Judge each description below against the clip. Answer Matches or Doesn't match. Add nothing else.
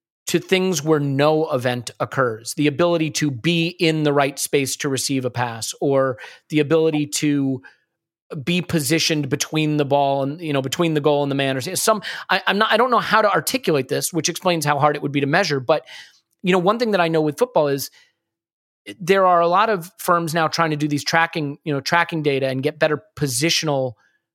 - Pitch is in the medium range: Matches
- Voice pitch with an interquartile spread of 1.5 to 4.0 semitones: Matches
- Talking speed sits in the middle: Doesn't match